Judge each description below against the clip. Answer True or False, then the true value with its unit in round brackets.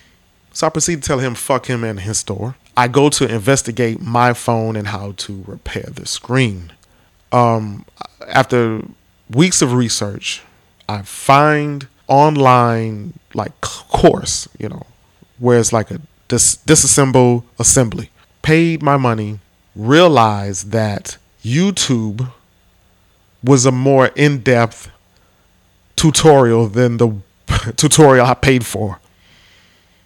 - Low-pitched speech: True (115 Hz)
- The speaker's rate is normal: False (120 wpm)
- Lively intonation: False (4.9 semitones)